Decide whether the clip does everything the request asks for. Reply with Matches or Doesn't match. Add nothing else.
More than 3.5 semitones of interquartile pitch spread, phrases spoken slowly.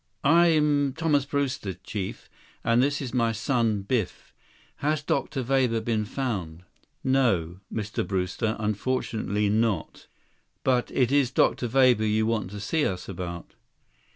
Matches